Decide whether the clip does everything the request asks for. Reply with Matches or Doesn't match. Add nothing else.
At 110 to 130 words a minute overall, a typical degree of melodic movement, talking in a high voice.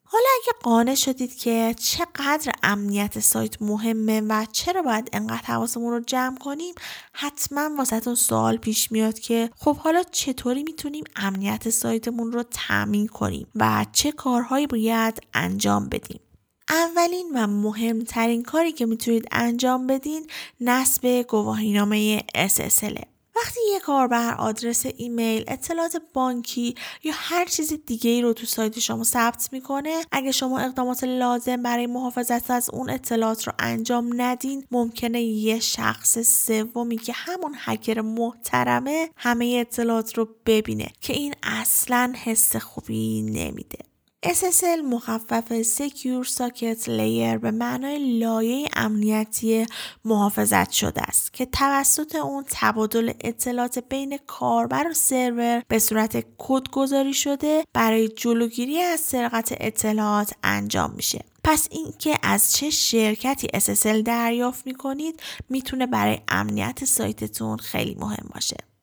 Matches